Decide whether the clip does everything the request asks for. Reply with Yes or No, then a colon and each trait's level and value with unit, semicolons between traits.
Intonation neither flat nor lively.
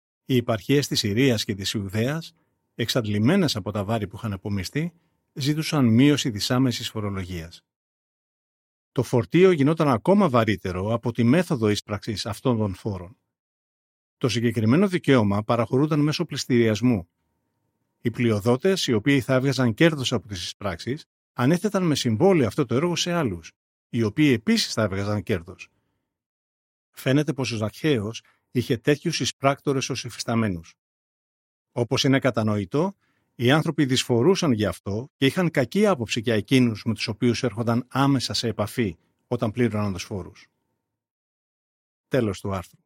Yes: average, 4.8 semitones